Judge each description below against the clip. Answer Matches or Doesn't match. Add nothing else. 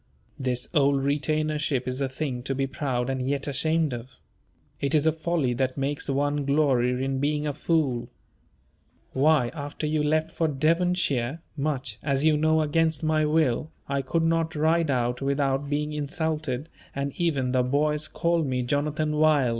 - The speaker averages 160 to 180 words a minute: Matches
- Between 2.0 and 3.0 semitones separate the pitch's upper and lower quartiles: Matches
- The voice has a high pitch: Doesn't match